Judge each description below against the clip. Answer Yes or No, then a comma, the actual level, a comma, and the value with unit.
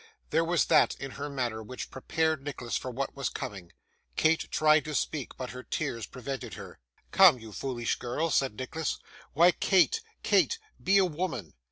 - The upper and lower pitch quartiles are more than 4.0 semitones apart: Yes, average, 4.5 semitones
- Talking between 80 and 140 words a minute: No, average, 175 wpm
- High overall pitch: No, low, 135 Hz